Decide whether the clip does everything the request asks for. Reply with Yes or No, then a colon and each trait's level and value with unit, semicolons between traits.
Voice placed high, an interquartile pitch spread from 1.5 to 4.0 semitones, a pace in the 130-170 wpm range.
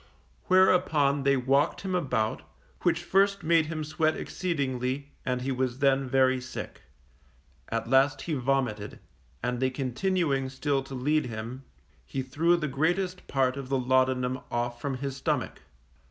No: low, 135 Hz; average, 3.5 semitones; average, 150 wpm